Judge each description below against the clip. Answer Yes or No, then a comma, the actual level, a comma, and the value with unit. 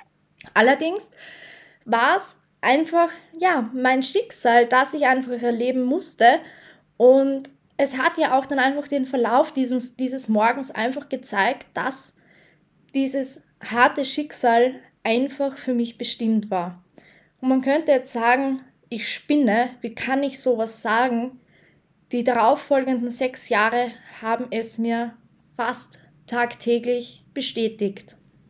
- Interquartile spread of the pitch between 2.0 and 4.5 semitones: Yes, narrow, 2.6 semitones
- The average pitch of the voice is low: No, very high, 255 Hz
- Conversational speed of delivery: No, slow, 120 wpm